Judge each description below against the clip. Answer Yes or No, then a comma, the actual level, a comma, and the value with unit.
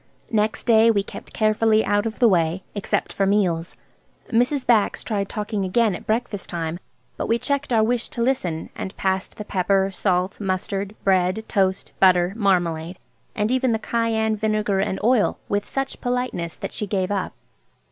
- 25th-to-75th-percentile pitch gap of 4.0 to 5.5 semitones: No, average, 3.1 semitones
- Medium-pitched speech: No, high, 205 Hz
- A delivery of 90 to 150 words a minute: No, average, 170 wpm